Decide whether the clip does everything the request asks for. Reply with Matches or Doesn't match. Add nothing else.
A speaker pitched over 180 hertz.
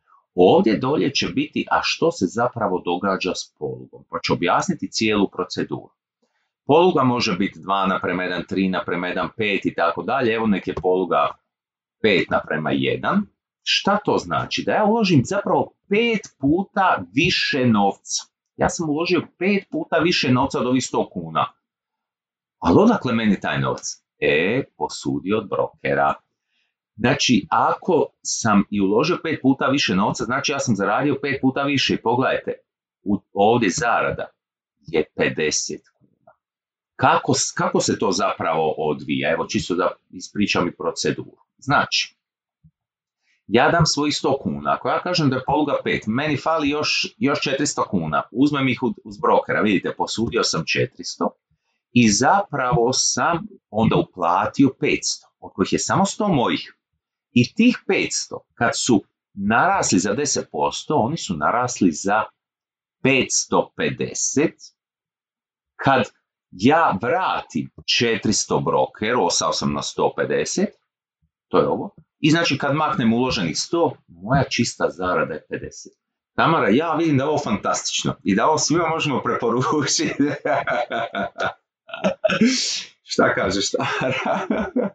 Doesn't match